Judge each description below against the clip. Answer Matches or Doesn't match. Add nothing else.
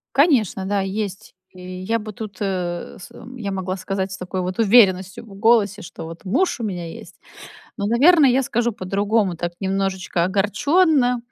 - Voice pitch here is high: Matches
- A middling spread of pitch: Matches